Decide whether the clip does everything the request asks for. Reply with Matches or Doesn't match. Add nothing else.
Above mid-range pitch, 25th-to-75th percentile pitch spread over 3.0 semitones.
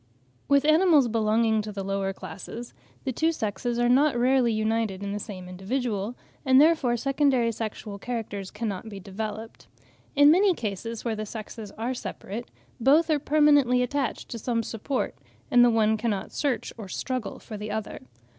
Matches